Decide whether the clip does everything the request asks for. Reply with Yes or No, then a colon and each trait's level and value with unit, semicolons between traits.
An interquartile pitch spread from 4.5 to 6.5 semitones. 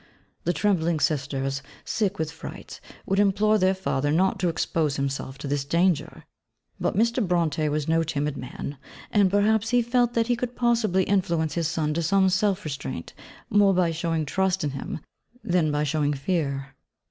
Yes: average, 5.1 semitones